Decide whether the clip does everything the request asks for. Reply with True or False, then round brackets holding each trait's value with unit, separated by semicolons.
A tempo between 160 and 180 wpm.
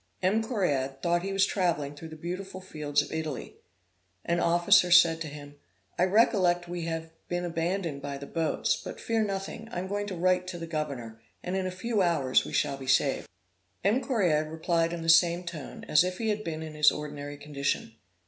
False (205 wpm)